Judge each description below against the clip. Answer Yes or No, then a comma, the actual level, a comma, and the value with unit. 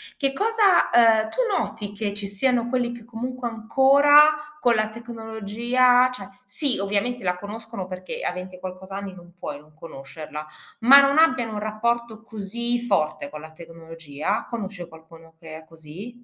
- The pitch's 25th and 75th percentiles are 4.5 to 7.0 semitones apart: Yes, average, 5.2 semitones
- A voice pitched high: Yes, high, 215 Hz